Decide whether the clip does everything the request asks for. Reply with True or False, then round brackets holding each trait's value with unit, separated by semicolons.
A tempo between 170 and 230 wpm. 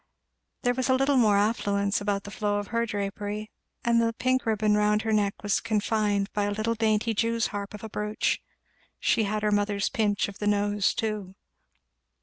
True (190 wpm)